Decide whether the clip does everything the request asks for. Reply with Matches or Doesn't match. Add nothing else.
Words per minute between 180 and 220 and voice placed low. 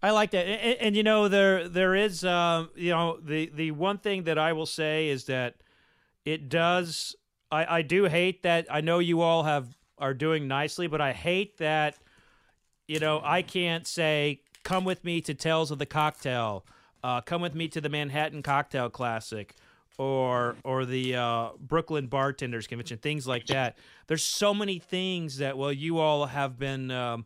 Doesn't match